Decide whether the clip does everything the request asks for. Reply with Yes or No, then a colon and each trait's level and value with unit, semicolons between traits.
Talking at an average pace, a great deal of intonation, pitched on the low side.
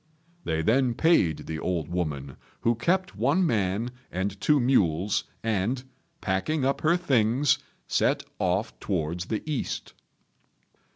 No: slow, 125 wpm; wide, 7.2 semitones; low, 110 Hz